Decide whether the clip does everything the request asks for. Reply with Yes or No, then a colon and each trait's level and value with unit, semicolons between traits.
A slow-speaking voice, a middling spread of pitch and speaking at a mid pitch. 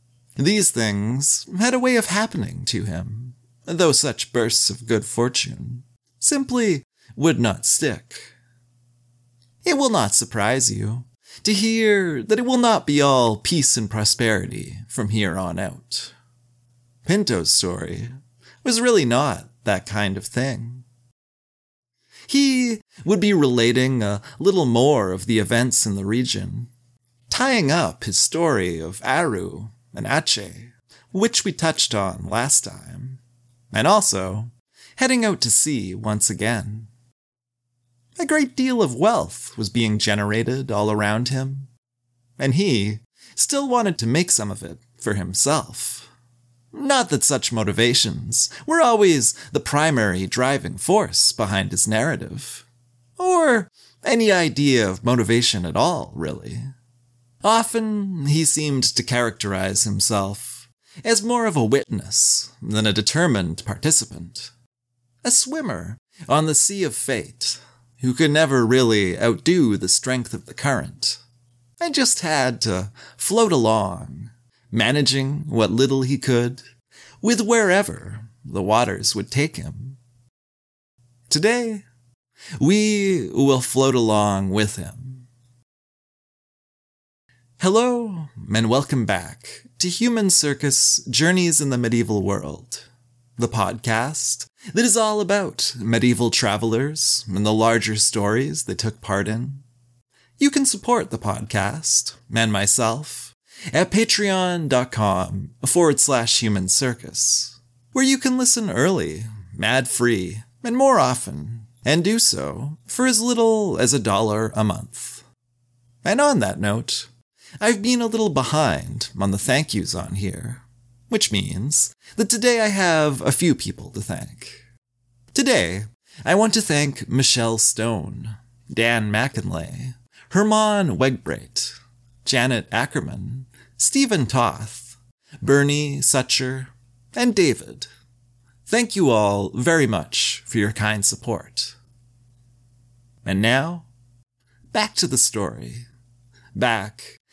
No: slow, 125 wpm; average, 4.8 semitones; low, 120 Hz